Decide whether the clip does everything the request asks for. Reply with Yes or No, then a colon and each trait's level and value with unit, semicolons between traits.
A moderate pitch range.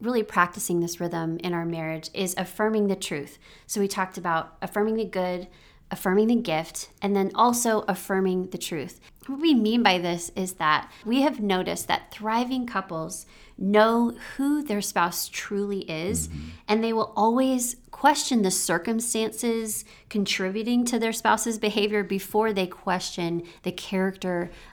Yes: average, 3.8 semitones